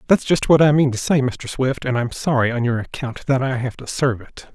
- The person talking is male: Yes, male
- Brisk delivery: Yes, fast, 275 wpm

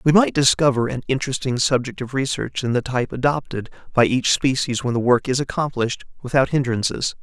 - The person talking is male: Yes, male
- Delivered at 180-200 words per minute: Yes, average, 185 wpm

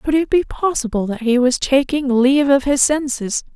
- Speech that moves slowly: No, fast, 205 wpm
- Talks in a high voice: Yes, very high, 270 Hz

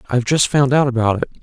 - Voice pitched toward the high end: No, low, 130 Hz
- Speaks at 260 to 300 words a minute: Yes, fast, 295 wpm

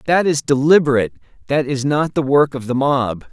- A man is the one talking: Yes, male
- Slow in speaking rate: No, average, 200 wpm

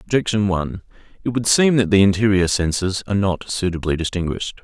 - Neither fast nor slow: Yes, average, 170 wpm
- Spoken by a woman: No, male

